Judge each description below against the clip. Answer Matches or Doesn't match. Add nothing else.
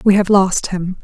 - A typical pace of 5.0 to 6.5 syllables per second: Doesn't match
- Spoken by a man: Doesn't match